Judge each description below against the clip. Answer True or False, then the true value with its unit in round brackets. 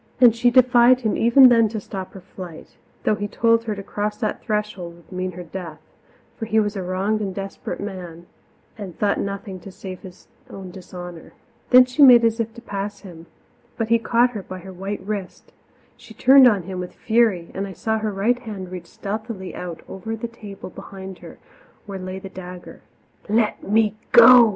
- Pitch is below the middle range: False (200 Hz)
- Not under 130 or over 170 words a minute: False (200 wpm)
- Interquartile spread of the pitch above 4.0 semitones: False (3.4 semitones)